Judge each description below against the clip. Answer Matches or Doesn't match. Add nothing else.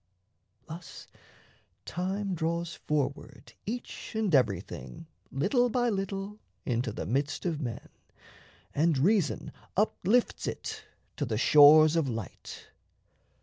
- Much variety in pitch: Matches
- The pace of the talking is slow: Matches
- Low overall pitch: Doesn't match